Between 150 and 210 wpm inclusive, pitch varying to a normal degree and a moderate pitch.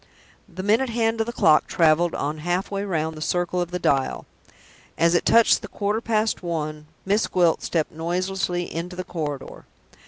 Yes: average, 175 wpm; average, 3.9 semitones; medium, 175 Hz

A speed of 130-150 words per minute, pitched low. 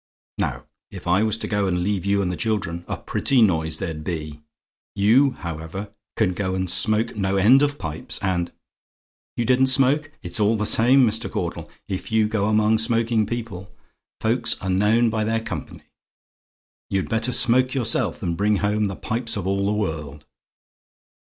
No: average, 175 wpm; low, 105 Hz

